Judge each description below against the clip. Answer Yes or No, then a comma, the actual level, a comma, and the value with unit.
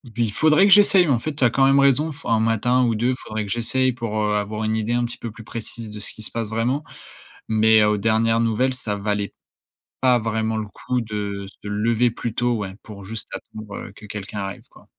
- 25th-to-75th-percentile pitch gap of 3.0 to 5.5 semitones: No, narrow, 2.6 semitones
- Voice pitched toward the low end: Yes, low, 115 Hz